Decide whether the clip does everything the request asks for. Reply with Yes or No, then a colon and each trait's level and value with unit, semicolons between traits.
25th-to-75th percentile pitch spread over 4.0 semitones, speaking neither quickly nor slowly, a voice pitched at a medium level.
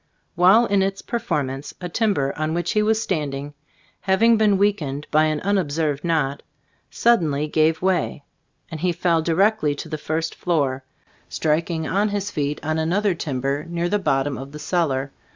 Yes: average, 4.7 semitones; average, 175 wpm; medium, 160 Hz